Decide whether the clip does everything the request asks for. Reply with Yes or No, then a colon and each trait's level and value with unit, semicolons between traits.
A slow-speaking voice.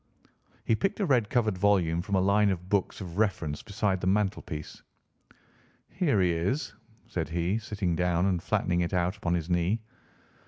No: average, 170 wpm